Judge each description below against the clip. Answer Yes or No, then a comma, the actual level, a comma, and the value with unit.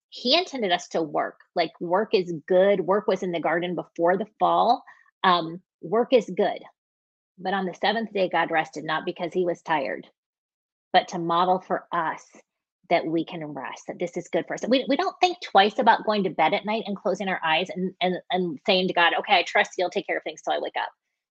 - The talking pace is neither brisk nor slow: No, fast, 230 wpm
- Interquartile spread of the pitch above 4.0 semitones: No, average, 2.8 semitones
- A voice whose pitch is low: No, medium, 185 Hz